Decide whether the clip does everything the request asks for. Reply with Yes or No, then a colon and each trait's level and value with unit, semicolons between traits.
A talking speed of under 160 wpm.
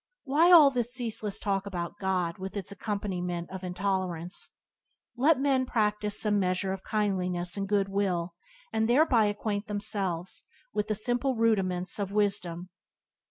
Yes: average, 145 wpm